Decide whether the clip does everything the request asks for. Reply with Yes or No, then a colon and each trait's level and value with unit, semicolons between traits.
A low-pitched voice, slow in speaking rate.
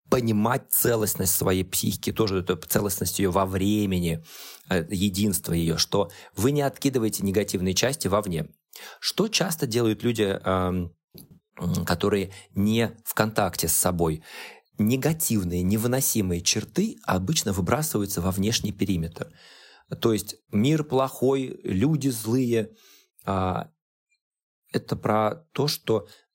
Yes: low, 105 Hz; slow, 105 wpm